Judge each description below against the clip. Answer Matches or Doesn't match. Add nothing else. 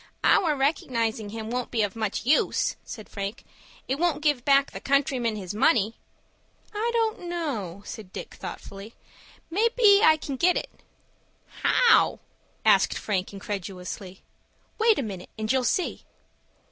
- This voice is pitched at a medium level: Doesn't match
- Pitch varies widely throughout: Matches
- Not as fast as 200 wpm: Matches